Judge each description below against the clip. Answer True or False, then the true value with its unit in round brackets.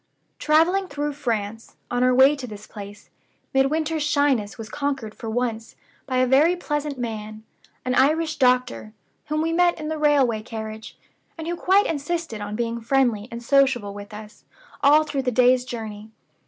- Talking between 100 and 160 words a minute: False (170 wpm)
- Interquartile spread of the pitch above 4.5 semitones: True (5.1 semitones)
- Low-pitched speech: False (255 Hz)